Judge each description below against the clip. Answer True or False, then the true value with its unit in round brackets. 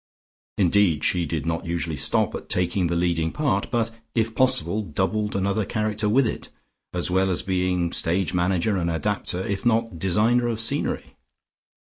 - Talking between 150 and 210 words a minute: True (160 wpm)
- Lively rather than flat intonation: False (3.9 semitones)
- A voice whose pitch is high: False (95 Hz)